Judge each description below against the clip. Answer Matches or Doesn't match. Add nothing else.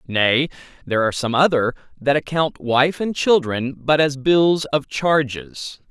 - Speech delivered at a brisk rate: Doesn't match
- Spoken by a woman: Doesn't match